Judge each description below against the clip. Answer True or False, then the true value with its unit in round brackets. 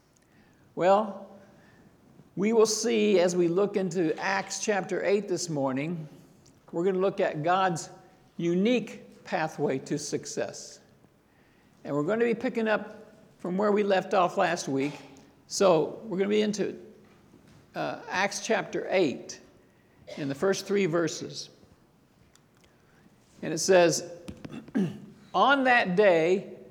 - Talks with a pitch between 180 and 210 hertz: True (190 Hz)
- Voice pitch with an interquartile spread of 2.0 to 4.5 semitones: True (3.4 semitones)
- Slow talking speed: True (130 wpm)